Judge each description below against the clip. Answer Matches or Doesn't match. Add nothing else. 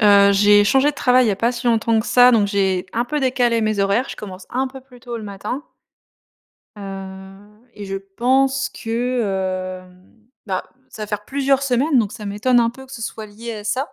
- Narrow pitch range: Doesn't match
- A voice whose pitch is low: Doesn't match